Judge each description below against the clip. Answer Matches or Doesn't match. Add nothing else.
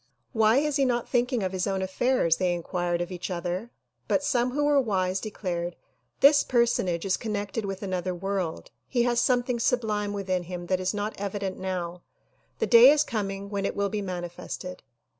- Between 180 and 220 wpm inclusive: Matches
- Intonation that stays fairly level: Doesn't match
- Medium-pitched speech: Doesn't match